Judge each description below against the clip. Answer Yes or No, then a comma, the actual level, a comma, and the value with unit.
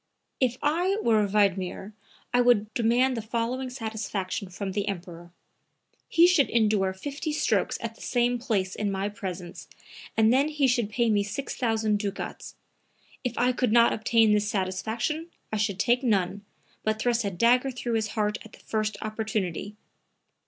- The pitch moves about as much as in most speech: Yes, average, 3.2 semitones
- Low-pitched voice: No, high, 220 Hz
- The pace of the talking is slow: No, average, 160 wpm